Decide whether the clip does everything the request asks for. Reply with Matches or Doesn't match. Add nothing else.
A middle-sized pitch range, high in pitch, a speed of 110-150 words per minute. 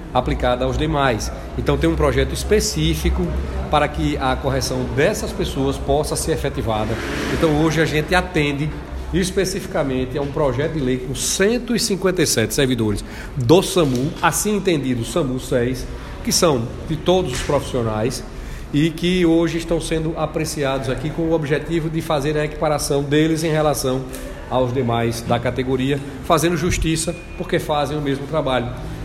Doesn't match